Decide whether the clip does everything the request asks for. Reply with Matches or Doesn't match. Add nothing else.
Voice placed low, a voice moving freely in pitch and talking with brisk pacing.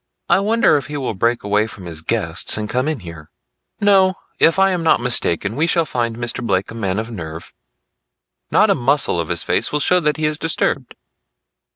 Matches